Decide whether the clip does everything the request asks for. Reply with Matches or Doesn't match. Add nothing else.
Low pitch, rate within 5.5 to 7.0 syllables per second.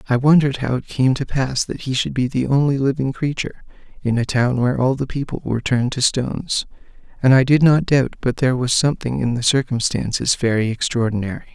Matches